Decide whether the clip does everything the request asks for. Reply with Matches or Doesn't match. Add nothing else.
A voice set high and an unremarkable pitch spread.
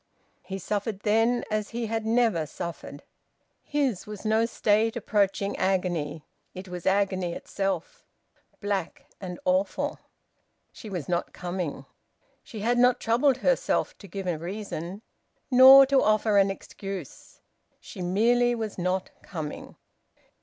Matches